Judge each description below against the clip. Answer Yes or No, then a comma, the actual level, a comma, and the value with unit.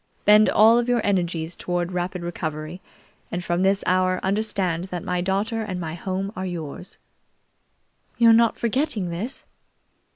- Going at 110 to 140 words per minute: No, average, 150 wpm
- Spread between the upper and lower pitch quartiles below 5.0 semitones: Yes, average, 3.4 semitones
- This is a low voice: No, medium, 185 Hz